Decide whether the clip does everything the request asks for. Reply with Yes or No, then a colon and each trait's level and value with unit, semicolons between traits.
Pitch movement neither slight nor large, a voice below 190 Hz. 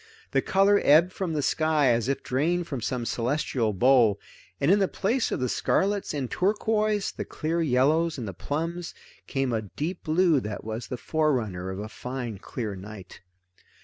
No: wide, 6.5 semitones; medium, 140 Hz